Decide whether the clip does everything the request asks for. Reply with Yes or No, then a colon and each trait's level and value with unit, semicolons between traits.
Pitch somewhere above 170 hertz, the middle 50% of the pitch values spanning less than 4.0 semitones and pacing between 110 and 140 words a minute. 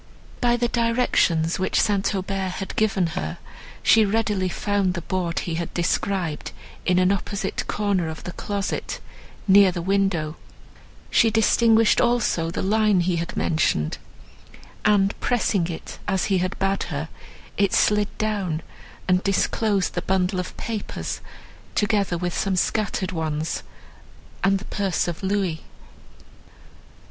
Yes: high, 190 Hz; average, 2.8 semitones; slow, 135 wpm